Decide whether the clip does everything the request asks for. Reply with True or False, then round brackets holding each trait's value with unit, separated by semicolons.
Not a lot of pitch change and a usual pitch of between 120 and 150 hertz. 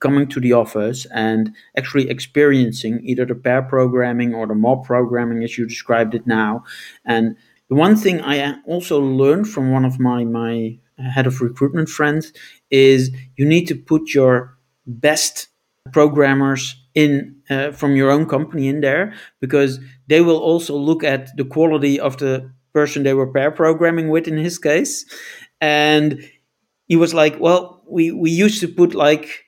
False (3.4 semitones; 140 Hz)